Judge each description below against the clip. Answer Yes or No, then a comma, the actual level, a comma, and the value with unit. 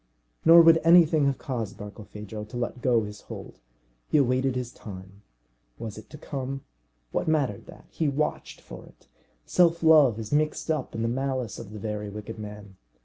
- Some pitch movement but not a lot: No, wide, 6.0 semitones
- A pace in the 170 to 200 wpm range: Yes, average, 180 wpm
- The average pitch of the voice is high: No, low, 125 Hz